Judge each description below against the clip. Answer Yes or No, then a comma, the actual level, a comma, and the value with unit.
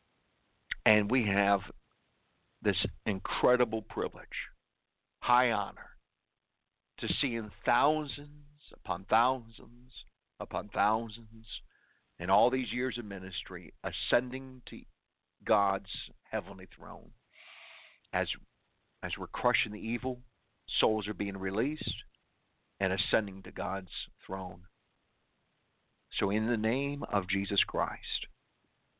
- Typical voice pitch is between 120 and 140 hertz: No, low, 110 Hz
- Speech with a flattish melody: No, average, 4.0 semitones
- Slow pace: Yes, slow, 100 wpm